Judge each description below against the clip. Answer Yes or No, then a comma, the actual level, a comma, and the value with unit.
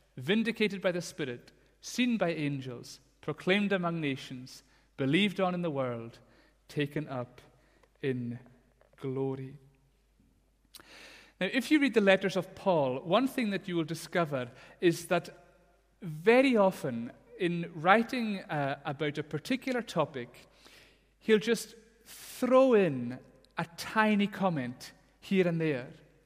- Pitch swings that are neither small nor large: No, wide, 6.3 semitones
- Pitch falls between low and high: Yes, medium, 170 Hz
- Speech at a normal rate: No, slow, 125 wpm